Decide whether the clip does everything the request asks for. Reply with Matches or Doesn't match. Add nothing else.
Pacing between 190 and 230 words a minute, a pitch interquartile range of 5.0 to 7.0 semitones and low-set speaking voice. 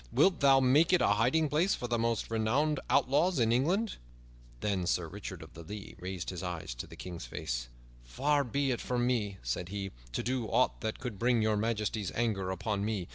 Matches